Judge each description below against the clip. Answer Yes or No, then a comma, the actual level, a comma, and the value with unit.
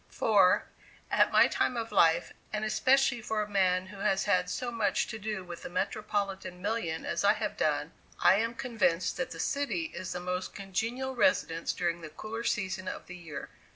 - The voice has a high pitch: Yes, high, 200 Hz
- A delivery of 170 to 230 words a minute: Yes, average, 190 wpm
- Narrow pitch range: No, average, 4.0 semitones